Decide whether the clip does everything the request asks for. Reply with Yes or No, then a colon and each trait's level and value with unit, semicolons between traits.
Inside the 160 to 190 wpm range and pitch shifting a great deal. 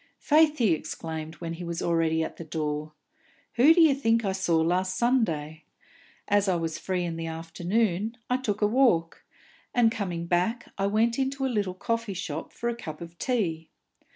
Yes: average, 180 wpm; wide, 5.9 semitones